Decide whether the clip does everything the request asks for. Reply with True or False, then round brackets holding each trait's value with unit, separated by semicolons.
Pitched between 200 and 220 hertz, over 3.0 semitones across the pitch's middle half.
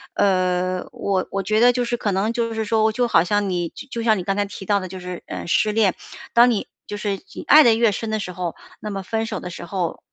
True (205 Hz; 3.4 semitones)